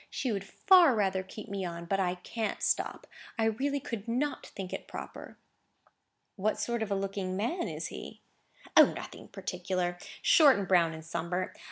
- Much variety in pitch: No, average, 4.2 semitones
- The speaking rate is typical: Yes, average, 175 wpm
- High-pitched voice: Yes, high, 195 Hz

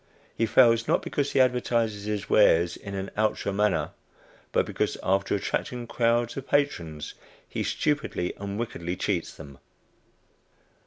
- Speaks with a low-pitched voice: Yes, low, 105 Hz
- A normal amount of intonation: Yes, average, 3.7 semitones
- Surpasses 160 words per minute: No, average, 140 wpm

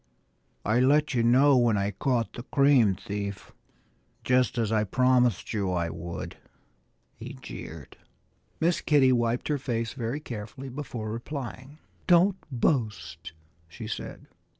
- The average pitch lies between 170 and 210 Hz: No, low, 120 Hz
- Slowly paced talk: Yes, slow, 130 wpm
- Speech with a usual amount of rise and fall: Yes, average, 4.6 semitones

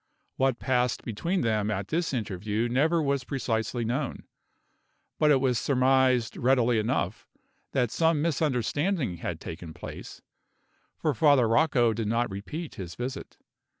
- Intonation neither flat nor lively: Yes, average, 4.1 semitones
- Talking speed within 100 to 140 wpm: Yes, slow, 135 wpm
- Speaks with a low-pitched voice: Yes, low, 125 Hz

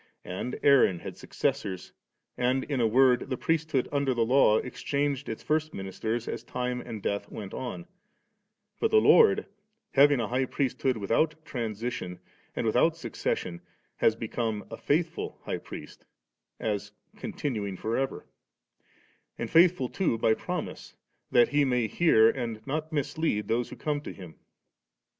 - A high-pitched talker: No, low, 125 Hz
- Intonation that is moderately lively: Yes, average, 4.6 semitones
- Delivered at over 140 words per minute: Yes, average, 150 wpm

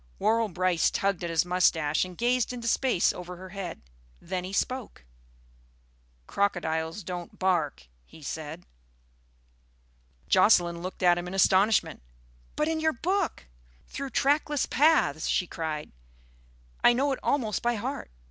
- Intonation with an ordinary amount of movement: No, wide, 5.8 semitones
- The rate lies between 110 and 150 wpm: Yes, average, 140 wpm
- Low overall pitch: No, medium, 185 Hz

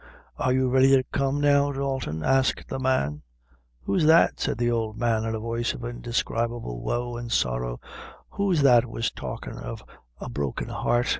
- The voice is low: Yes, low, 120 Hz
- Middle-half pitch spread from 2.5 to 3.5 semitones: Yes, average, 3.0 semitones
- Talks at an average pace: Yes, average, 170 wpm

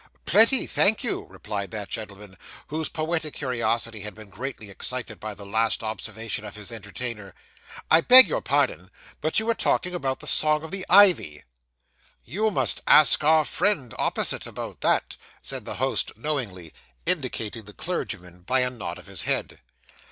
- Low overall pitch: Yes, low, 120 Hz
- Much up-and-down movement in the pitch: Yes, wide, 7.2 semitones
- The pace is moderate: Yes, average, 165 wpm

